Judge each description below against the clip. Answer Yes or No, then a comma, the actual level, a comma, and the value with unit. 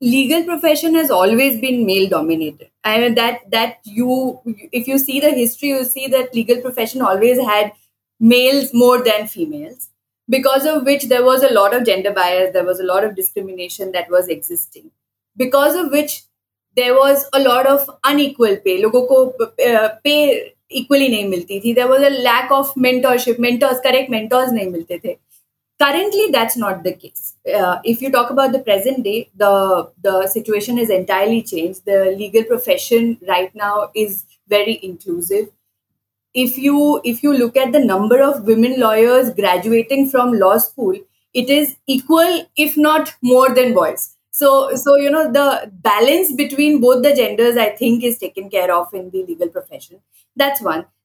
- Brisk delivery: No, average, 170 wpm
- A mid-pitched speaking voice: No, very high, 250 Hz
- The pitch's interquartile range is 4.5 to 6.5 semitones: Yes, average, 5.1 semitones